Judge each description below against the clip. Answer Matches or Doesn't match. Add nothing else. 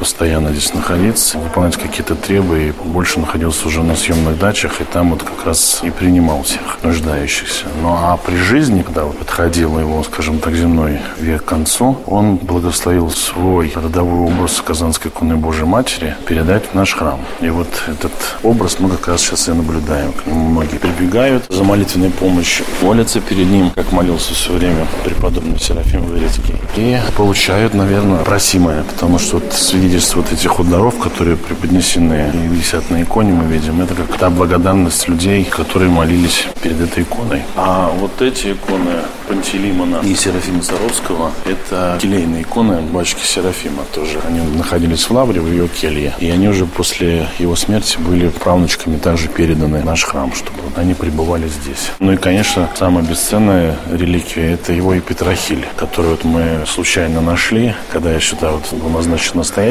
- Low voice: Matches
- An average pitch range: Doesn't match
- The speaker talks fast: Matches